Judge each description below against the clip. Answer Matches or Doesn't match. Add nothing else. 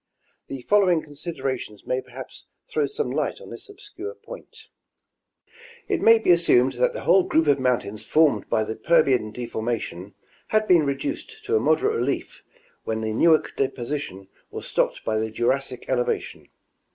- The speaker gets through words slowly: Doesn't match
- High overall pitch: Doesn't match